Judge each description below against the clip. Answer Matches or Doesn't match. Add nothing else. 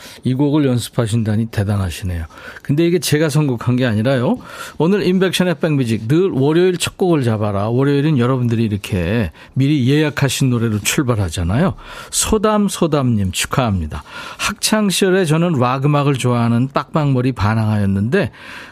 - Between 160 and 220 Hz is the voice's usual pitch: Doesn't match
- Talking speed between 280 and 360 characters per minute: Matches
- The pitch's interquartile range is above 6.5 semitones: Doesn't match